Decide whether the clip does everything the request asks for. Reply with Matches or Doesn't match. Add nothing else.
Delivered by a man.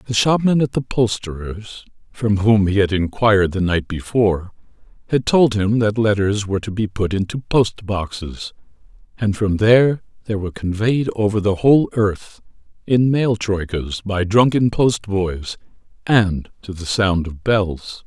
Matches